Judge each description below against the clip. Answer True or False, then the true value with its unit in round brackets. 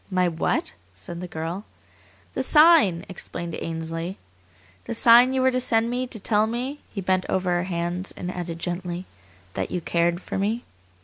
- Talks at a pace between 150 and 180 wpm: True (175 wpm)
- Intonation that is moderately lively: True (5.0 semitones)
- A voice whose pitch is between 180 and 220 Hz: True (185 Hz)